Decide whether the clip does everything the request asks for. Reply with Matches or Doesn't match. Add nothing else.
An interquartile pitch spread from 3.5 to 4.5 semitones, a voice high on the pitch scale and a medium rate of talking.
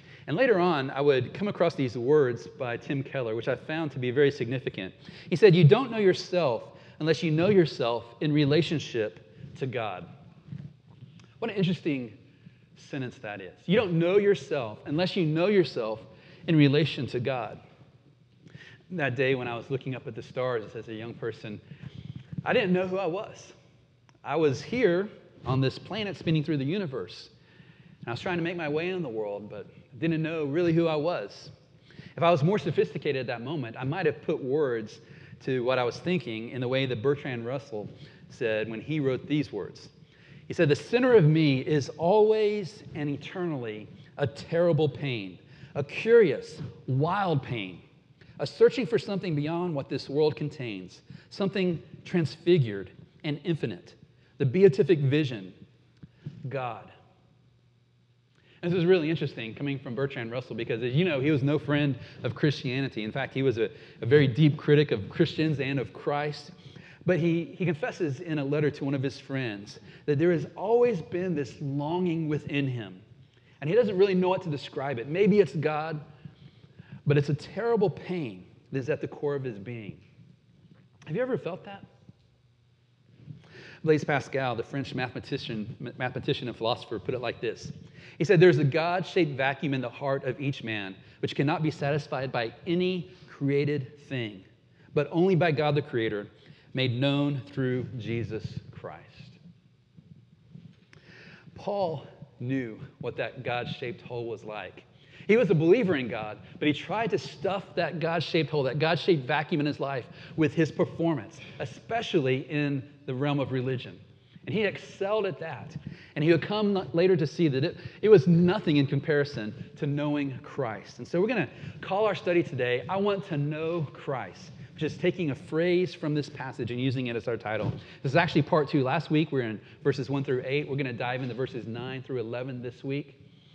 Doesn't match